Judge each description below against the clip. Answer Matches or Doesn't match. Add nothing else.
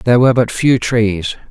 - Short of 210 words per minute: Matches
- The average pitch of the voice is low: Matches